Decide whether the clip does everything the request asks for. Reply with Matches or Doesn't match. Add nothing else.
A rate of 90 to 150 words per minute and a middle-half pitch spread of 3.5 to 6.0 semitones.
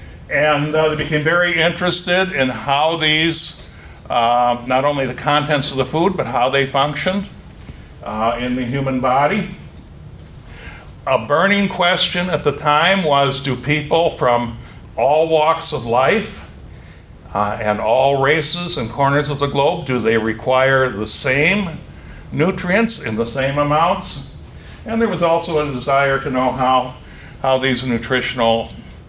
Matches